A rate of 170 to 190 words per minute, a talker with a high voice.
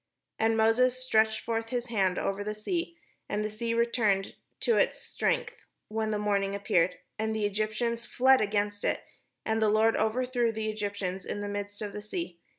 Yes: average, 180 wpm; high, 215 Hz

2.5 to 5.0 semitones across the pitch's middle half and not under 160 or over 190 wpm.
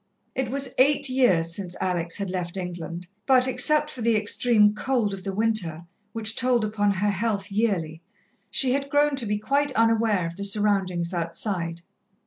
No: wide, 5.4 semitones; average, 170 wpm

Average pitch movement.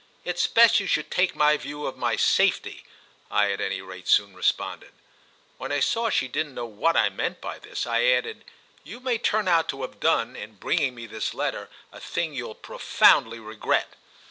No: wide, 8.4 semitones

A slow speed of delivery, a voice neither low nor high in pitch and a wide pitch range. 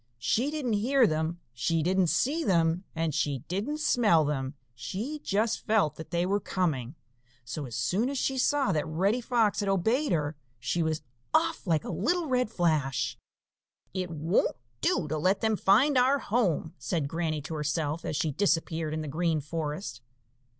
No: average, 175 wpm; medium, 170 Hz; wide, 6.3 semitones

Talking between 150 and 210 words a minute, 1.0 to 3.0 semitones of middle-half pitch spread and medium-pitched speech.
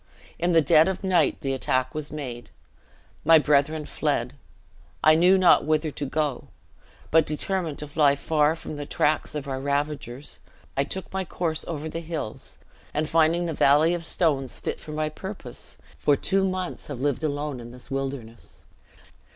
Yes: average, 170 wpm; average, 2.7 semitones; medium, 150 Hz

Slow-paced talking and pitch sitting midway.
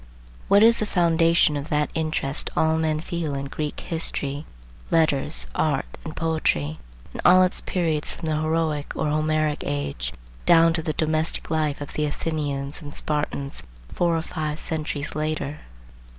No: average, 155 wpm; medium, 155 Hz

